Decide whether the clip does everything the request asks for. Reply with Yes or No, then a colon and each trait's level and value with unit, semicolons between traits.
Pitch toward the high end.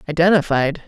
No: medium, 160 Hz